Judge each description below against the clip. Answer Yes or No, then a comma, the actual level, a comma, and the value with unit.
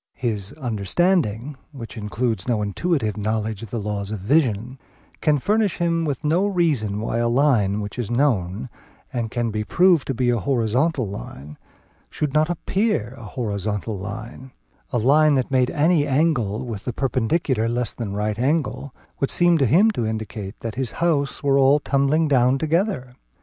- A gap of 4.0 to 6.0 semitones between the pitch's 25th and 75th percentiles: Yes, wide, 5.6 semitones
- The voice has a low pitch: Yes, low, 125 Hz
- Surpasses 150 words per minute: Yes, average, 170 wpm